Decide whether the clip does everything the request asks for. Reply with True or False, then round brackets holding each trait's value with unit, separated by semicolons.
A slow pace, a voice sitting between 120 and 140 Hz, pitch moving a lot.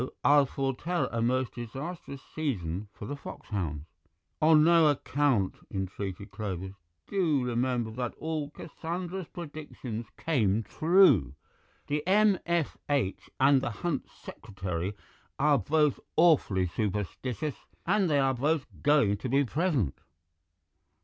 True (115 wpm; 135 Hz; 6.6 semitones)